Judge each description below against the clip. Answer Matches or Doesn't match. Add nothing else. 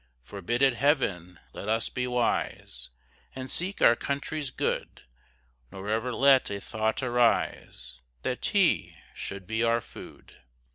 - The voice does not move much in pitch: Doesn't match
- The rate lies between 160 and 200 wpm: Doesn't match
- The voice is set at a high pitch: Doesn't match